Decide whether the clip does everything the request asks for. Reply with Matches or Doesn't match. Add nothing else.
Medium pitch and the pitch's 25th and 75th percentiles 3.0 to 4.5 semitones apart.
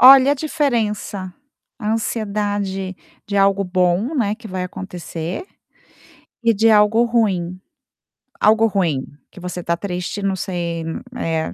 Doesn't match